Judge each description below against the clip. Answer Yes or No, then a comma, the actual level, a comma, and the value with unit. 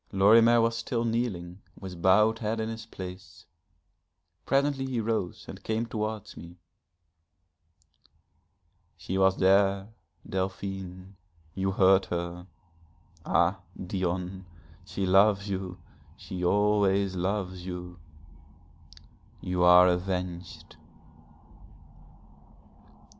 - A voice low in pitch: Yes, very low, 95 Hz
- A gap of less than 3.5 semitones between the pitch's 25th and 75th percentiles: Yes, average, 2.7 semitones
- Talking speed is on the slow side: Yes, slow, 95 wpm